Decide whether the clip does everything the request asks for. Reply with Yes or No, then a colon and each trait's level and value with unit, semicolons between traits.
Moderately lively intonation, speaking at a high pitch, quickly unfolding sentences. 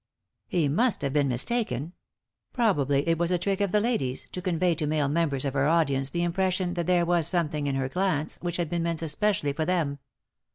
No: average, 4.0 semitones; medium, 165 Hz; fast, 210 wpm